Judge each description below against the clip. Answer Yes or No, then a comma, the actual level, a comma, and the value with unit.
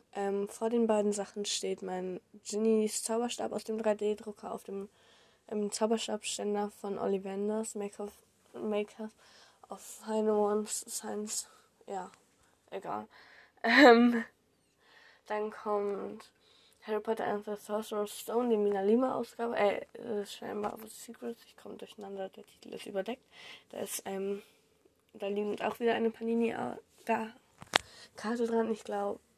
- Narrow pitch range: Yes, narrow, 1.7 semitones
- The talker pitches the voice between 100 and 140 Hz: No, high, 215 Hz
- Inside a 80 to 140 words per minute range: Yes, average, 135 wpm